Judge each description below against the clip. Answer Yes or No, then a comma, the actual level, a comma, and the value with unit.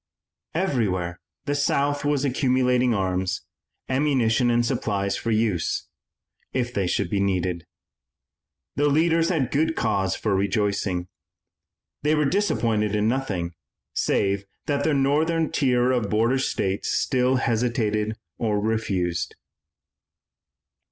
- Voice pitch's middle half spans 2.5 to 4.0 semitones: No, wide, 5.6 semitones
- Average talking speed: No, slow, 115 wpm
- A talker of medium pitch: No, low, 115 Hz